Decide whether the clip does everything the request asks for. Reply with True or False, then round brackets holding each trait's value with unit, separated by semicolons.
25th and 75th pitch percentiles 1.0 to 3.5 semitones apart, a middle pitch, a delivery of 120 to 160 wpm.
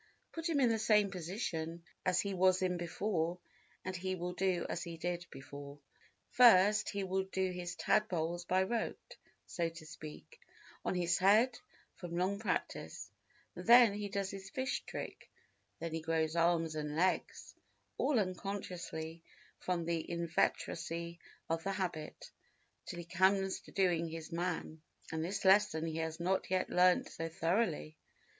True (2.8 semitones; 180 Hz; 155 wpm)